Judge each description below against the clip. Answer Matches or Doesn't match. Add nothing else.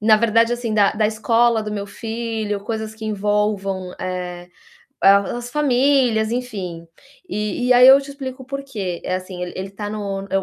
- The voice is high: Matches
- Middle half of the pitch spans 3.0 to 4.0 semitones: Matches